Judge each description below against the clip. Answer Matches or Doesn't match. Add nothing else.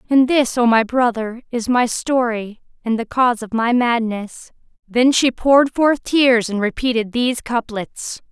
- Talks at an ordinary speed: Matches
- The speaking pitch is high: Matches